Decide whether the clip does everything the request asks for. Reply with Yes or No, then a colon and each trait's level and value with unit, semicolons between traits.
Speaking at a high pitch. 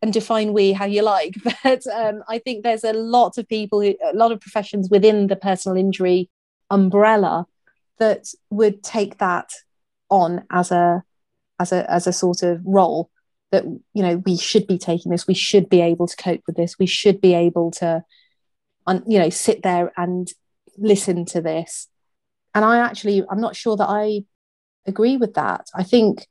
Yes: high, 195 Hz